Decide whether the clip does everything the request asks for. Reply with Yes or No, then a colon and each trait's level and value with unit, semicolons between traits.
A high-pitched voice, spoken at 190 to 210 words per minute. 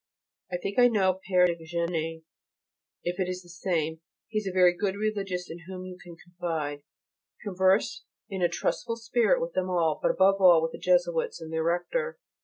No: medium, 180 Hz; average, 195 wpm